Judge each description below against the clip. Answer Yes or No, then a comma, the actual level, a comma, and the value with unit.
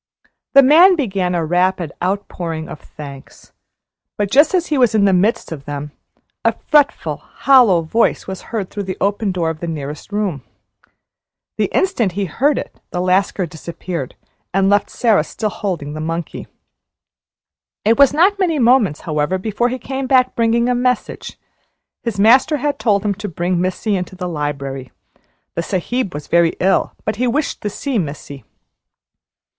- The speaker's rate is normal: Yes, average, 165 wpm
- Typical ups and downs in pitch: No, wide, 6.4 semitones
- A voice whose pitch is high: Yes, high, 195 Hz